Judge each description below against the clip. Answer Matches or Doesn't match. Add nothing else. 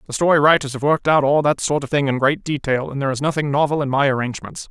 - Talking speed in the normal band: Doesn't match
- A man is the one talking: Matches